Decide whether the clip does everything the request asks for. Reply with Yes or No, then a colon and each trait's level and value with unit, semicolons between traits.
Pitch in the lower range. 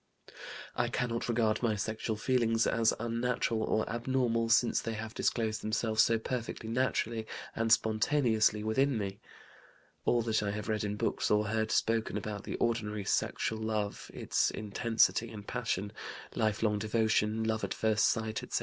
Yes: low, 110 Hz